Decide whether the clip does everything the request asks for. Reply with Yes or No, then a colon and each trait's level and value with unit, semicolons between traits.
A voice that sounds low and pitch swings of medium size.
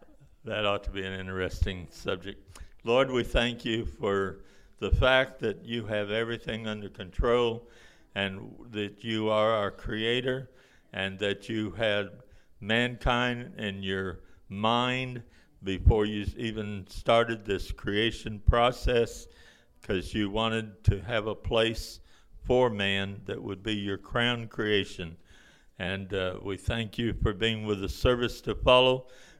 Yes: low, 105 Hz; average, 3.2 semitones